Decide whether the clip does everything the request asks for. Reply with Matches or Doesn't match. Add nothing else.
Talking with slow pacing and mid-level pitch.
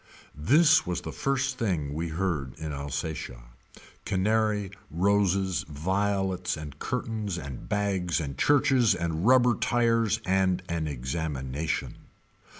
Doesn't match